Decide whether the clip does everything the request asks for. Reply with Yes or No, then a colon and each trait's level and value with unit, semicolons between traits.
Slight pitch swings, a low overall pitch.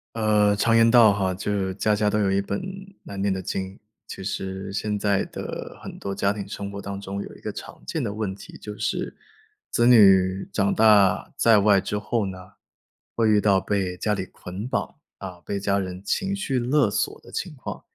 Yes: narrow, 1.8 semitones; low, 100 Hz